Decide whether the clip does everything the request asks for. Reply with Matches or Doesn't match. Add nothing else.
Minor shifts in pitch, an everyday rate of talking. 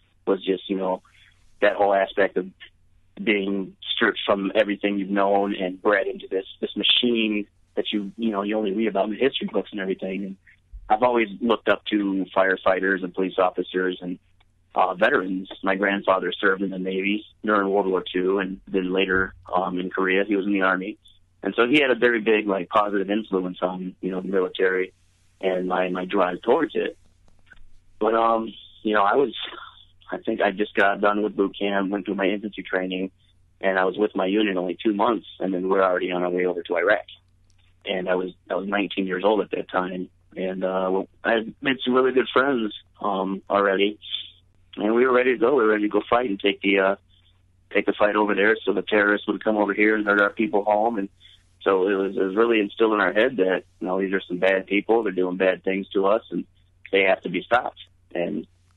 Doesn't match